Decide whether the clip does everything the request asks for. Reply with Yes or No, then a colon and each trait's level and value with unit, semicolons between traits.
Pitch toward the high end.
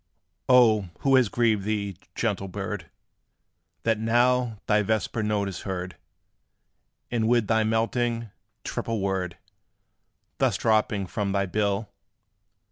No: low, 110 Hz